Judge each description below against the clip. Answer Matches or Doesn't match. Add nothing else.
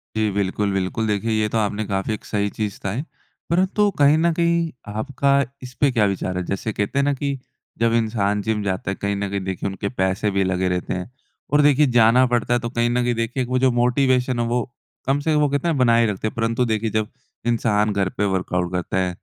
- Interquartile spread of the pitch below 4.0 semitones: Doesn't match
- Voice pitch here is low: Matches